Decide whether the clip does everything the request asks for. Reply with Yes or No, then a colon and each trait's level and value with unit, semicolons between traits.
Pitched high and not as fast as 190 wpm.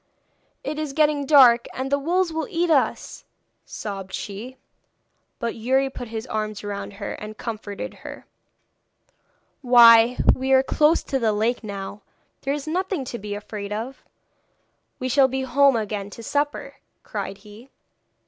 Yes: high, 245 Hz; average, 150 wpm